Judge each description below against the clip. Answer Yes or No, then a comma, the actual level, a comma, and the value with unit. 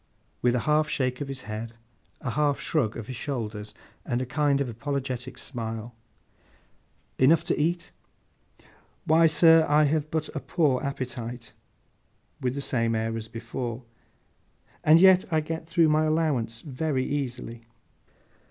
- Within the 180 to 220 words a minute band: No, average, 145 wpm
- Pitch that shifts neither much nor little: Yes, average, 4.6 semitones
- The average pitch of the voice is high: No, low, 135 Hz